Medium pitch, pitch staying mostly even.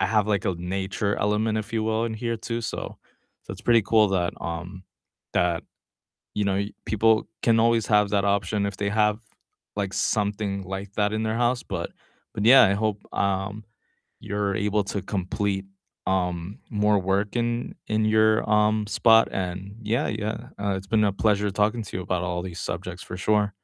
No: low, 105 Hz; narrow, 2.1 semitones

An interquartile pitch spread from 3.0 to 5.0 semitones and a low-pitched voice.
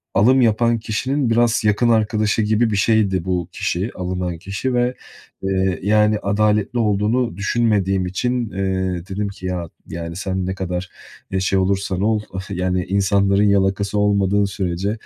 No: narrow, 2.5 semitones; low, 100 Hz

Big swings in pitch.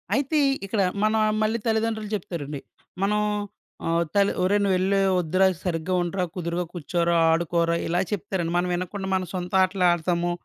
No: average, 2.7 semitones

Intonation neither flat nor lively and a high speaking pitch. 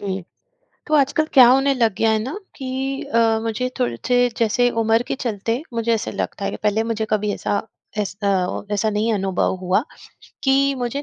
Yes: average, 3.7 semitones; high, 225 Hz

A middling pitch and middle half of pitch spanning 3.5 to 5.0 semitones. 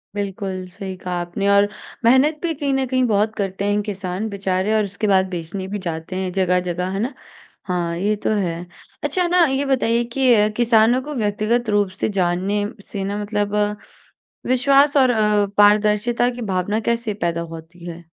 No: high, 205 Hz; average, 4.1 semitones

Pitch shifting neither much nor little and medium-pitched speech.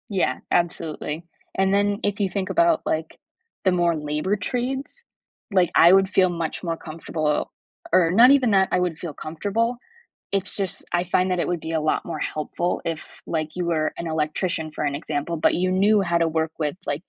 Yes: average, 3.4 semitones; medium, 175 Hz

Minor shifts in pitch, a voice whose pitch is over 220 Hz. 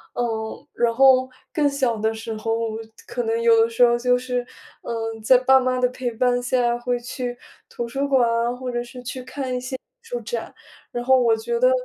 Yes: narrow, 1.7 semitones; high, 245 Hz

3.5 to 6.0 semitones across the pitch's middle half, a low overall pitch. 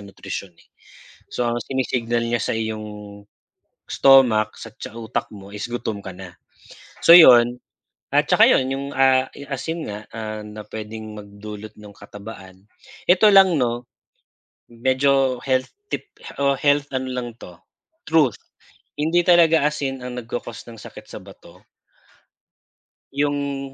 Yes: average, 4.3 semitones; low, 120 Hz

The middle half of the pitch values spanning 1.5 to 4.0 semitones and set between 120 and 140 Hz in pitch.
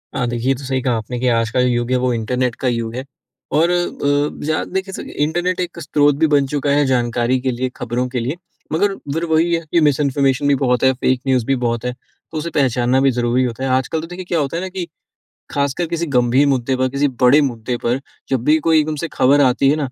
Yes: average, 3.5 semitones; low, 135 Hz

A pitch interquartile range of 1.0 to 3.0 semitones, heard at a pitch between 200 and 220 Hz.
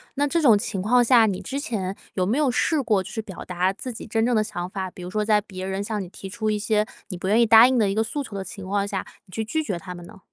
No: average, 3.4 semitones; high, 210 Hz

